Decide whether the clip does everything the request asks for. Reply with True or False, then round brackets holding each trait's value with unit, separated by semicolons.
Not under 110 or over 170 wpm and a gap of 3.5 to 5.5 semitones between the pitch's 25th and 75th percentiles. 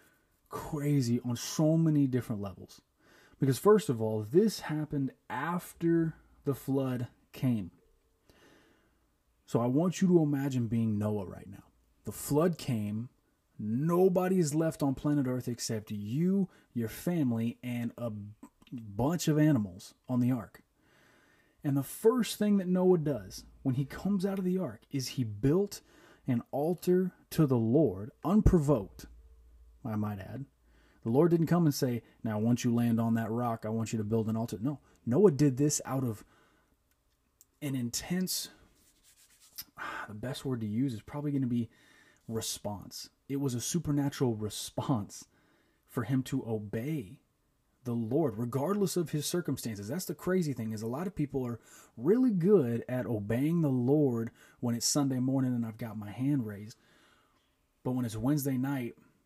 True (160 wpm; 5.0 semitones)